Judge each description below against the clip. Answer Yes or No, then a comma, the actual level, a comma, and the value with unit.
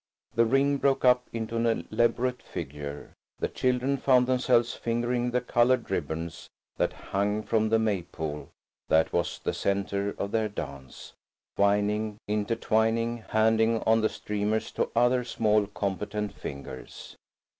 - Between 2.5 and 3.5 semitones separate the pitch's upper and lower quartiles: Yes, average, 2.9 semitones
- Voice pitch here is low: Yes, low, 110 Hz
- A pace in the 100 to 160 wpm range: Yes, slow, 135 wpm